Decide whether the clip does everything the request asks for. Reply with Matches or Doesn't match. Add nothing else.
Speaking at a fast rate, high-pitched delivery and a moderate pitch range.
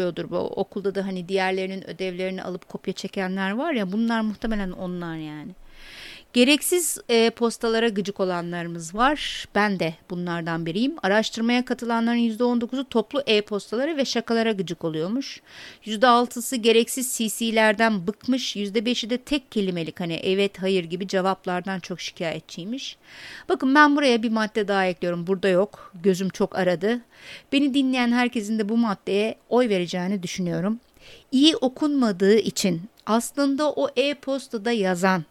Doesn't match